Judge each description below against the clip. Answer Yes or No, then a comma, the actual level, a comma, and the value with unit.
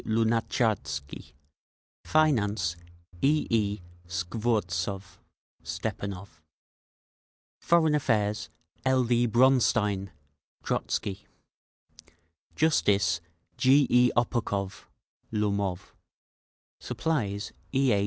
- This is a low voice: Yes, low, 110 Hz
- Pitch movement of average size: Yes, average, 4.1 semitones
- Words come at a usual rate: No, slow, 65 wpm